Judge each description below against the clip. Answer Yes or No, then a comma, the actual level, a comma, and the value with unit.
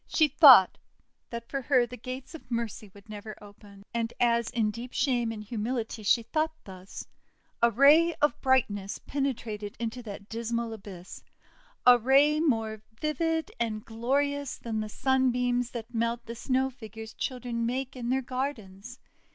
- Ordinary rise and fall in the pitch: Yes, average, 3.2 semitones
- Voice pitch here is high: Yes, high, 235 Hz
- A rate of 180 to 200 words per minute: No, average, 155 wpm